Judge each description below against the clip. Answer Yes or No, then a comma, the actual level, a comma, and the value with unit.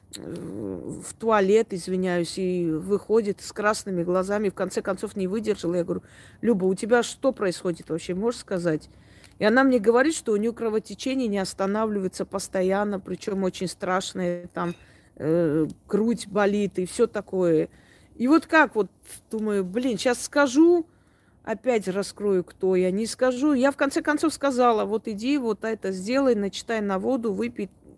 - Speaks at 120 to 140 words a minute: No, average, 155 wpm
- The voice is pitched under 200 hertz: No, high, 205 Hz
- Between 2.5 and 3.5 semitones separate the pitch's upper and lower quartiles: No, average, 3.9 semitones